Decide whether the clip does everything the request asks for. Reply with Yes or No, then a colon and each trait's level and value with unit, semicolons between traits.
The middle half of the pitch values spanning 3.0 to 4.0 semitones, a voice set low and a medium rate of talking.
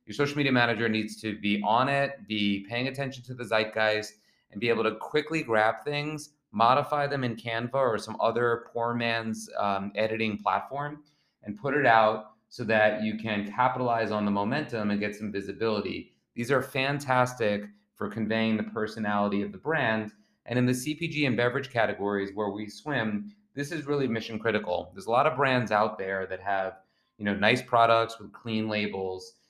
Yes: average, 3.4 semitones; low, 110 Hz; average, 185 wpm